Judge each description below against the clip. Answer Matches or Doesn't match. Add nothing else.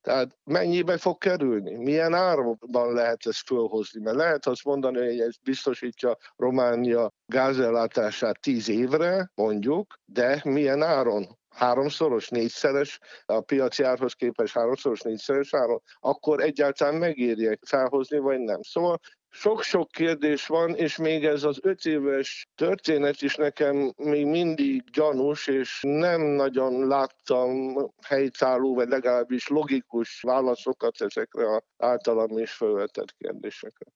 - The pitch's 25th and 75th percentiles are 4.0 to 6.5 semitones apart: Matches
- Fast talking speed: Doesn't match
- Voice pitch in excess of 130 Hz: Matches